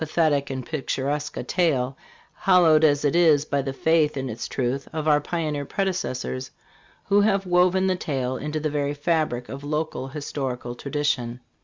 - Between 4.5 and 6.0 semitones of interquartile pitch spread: No, average, 3.3 semitones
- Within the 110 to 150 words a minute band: No, average, 165 wpm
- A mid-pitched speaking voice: Yes, medium, 150 Hz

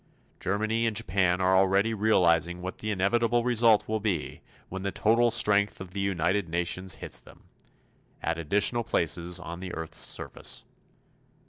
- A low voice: Yes, very low, 95 Hz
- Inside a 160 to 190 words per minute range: No, average, 150 wpm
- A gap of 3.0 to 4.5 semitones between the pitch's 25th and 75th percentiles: Yes, average, 3.7 semitones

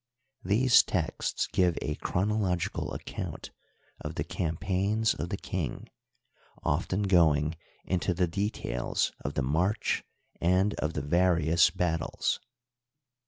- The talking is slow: Yes, slow, 115 wpm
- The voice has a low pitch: Yes, very low, 90 Hz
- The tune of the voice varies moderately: Yes, average, 3.3 semitones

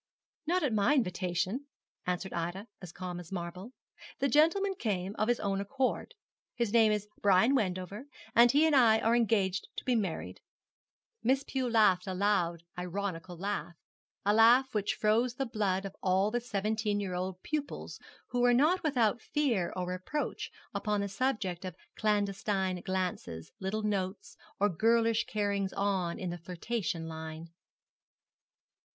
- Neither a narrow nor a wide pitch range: Yes, average, 4.2 semitones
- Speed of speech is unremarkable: Yes, average, 155 wpm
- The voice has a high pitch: Yes, high, 205 Hz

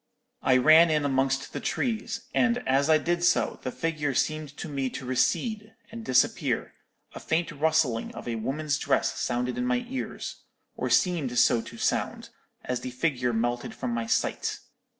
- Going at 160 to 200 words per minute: Yes, average, 170 wpm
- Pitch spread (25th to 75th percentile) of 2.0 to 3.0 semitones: No, average, 5.0 semitones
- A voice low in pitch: No, medium, 145 Hz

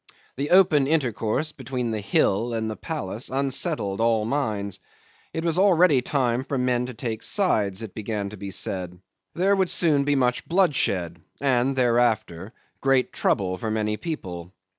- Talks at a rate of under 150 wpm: No, average, 160 wpm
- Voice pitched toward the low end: Yes, low, 120 Hz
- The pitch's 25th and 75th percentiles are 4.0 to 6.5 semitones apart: Yes, average, 5.2 semitones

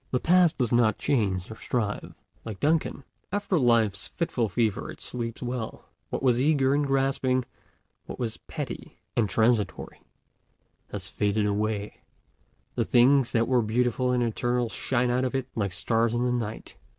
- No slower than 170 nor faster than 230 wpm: No, average, 160 wpm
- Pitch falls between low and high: No, low, 120 Hz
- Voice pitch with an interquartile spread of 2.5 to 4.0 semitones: Yes, average, 2.8 semitones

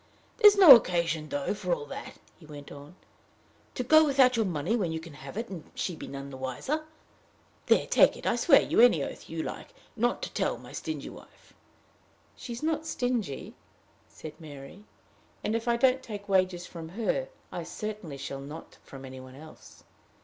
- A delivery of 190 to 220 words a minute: Yes, average, 195 wpm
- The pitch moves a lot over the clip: Yes, wide, 8.5 semitones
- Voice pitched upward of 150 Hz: Yes, medium, 185 Hz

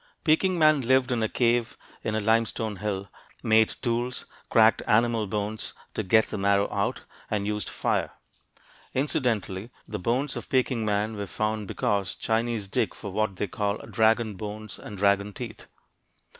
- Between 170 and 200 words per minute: No, average, 155 wpm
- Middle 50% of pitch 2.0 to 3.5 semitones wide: Yes, narrow, 2.4 semitones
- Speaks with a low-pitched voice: Yes, low, 110 Hz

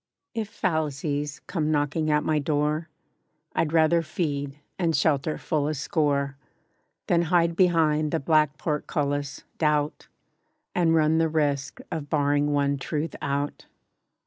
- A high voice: No, medium, 150 Hz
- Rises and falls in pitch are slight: Yes, narrow, 2.0 semitones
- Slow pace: Yes, slow, 130 wpm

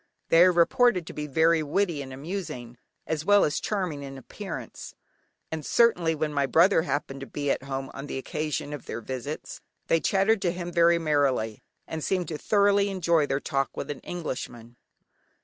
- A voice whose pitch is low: No, medium, 155 Hz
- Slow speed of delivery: No, average, 185 wpm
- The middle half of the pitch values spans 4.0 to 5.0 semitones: Yes, average, 4.4 semitones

